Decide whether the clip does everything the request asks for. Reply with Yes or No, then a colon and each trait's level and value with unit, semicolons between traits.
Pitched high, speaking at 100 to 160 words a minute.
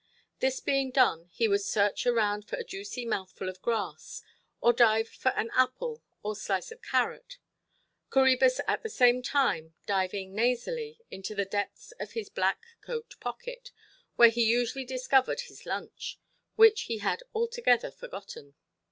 Yes: high, 245 Hz; average, 145 wpm